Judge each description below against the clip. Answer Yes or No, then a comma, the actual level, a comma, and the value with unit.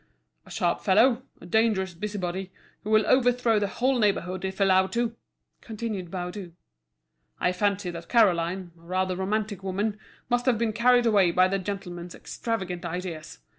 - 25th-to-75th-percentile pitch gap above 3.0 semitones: Yes, average, 3.5 semitones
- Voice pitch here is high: Yes, high, 195 Hz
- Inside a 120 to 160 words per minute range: Yes, average, 155 wpm